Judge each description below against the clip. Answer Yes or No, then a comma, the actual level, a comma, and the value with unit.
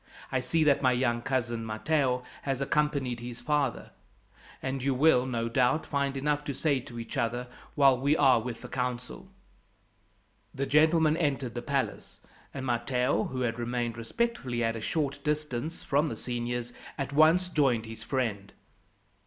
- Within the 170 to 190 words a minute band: No, average, 160 wpm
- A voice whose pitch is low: Yes, low, 130 Hz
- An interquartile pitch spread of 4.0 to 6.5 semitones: No, average, 3.2 semitones